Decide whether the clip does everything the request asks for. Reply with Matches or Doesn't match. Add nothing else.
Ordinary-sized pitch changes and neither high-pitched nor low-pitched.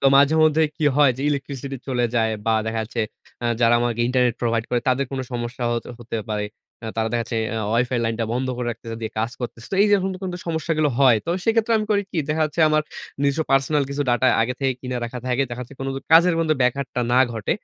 Doesn't match